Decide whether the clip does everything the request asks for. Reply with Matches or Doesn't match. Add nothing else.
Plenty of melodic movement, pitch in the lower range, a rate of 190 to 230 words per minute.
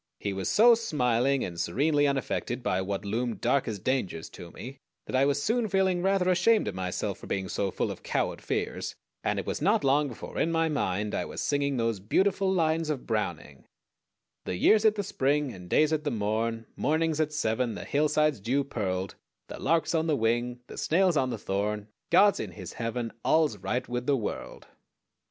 Matches